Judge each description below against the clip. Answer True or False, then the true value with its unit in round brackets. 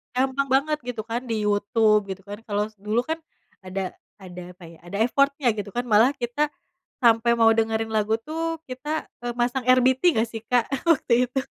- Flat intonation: False (3.4 semitones)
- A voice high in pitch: True (235 Hz)